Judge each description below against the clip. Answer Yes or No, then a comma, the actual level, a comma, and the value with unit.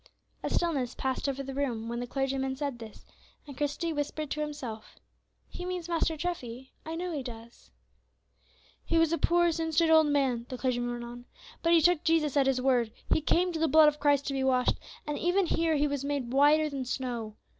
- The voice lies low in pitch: No, very high, 285 Hz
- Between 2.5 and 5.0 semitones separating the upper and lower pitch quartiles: Yes, average, 4.1 semitones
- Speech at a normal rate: No, fast, 210 wpm